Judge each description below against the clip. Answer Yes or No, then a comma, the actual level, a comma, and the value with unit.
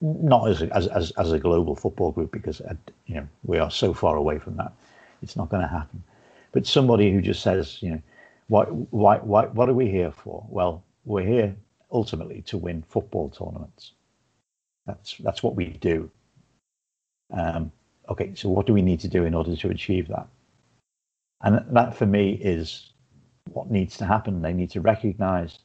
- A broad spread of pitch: No, average, 3.7 semitones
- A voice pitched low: Yes, low, 100 Hz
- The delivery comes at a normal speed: Yes, average, 185 wpm